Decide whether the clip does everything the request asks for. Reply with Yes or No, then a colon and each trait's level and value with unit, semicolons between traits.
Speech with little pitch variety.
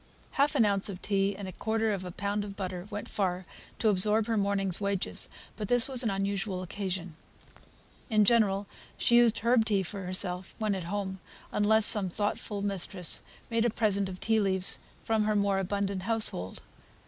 Yes: narrow, 2.3 semitones